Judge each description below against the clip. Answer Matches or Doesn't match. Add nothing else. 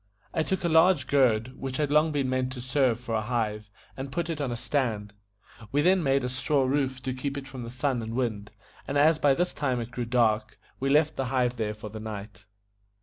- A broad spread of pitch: Doesn't match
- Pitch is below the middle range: Matches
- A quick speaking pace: Matches